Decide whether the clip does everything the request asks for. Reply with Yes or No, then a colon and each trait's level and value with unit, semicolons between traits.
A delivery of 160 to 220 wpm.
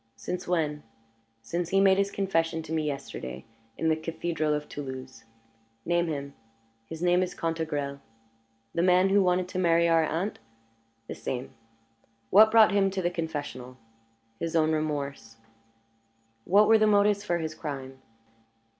No: average, 150 wpm